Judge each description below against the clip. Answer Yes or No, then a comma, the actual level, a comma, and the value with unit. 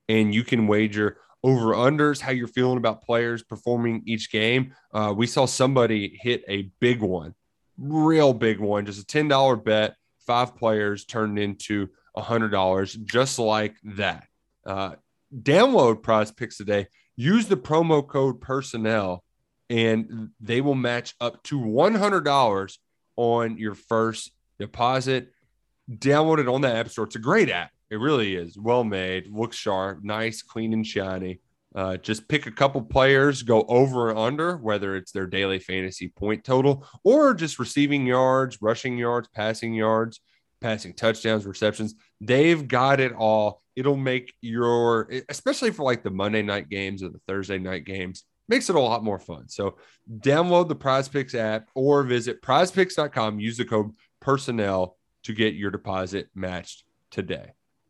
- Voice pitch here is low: Yes, low, 115 Hz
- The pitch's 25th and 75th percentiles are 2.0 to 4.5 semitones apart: Yes, average, 3.7 semitones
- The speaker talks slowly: No, average, 160 wpm